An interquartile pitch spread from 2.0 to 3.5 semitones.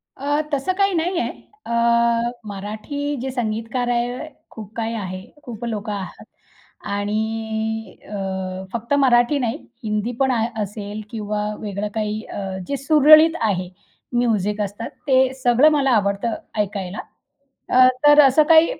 No: average, 4.0 semitones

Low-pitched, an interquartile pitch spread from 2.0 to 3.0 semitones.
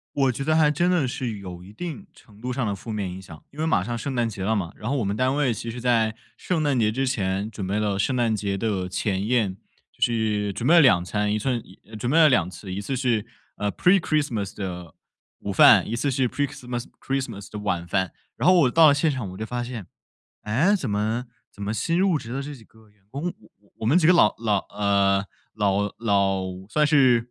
No: low, 115 Hz; average, 5.1 semitones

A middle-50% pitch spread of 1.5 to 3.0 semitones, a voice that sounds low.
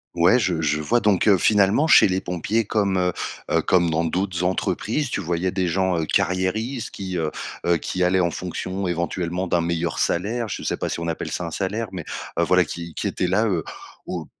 Yes: narrow, 2.6 semitones; very low, 90 Hz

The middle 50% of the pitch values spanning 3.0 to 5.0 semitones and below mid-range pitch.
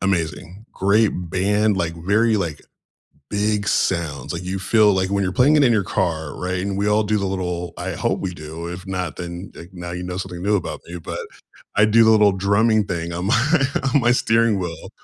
Yes: average, 3.3 semitones; very low, 95 Hz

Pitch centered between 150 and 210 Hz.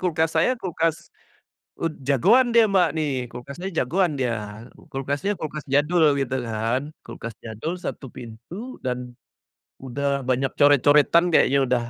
No: medium, 140 Hz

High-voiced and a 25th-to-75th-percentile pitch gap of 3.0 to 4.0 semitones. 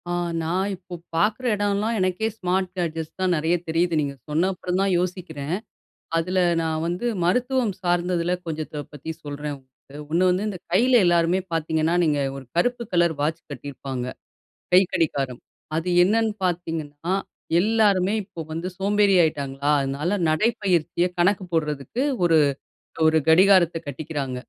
No: medium, 175 Hz; average, 3.4 semitones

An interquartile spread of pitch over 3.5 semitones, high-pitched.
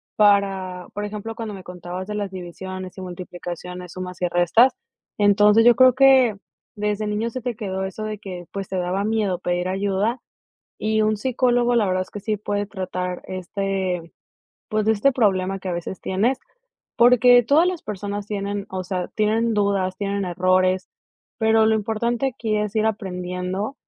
No: average, 2.9 semitones; high, 200 Hz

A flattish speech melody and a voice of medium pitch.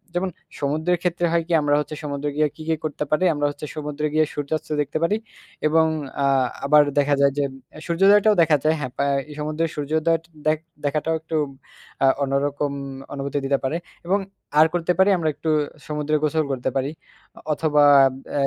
Yes: narrow, 2.0 semitones; medium, 150 Hz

